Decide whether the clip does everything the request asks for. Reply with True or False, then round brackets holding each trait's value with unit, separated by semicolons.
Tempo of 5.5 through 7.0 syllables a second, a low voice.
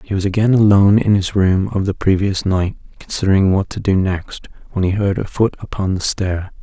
False (5.3 syllables/s; 95 Hz)